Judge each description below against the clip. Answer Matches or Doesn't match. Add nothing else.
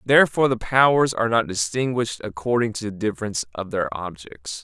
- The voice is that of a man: Matches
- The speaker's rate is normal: Matches